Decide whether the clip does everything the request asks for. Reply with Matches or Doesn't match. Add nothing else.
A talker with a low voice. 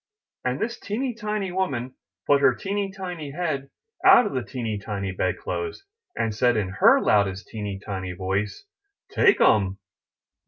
Matches